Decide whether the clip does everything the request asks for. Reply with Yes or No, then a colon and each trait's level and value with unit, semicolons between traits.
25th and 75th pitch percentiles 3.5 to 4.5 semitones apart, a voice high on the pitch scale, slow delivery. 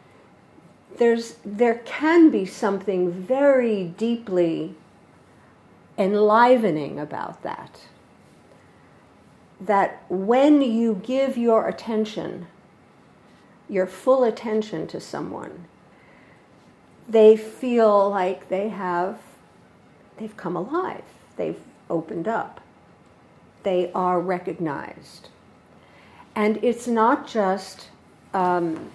Yes: average, 4.0 semitones; high, 210 Hz; slow, 85 wpm